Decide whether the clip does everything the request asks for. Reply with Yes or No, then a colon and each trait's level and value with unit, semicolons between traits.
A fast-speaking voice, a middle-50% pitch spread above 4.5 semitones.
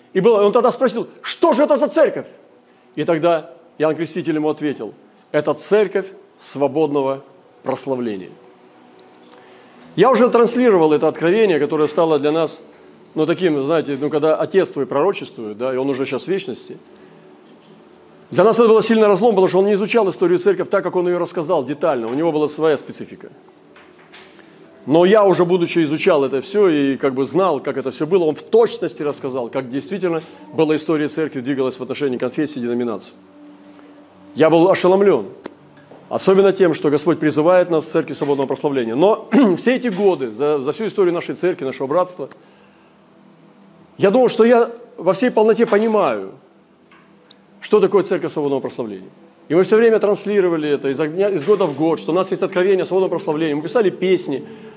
Yes: fast, 170 wpm; wide, 5.6 semitones